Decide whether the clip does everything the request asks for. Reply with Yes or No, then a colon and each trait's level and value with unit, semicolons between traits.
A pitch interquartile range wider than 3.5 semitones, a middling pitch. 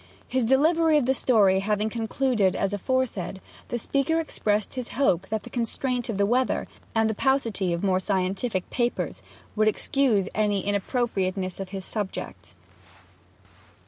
No: average, 4.7 semitones; high, 220 Hz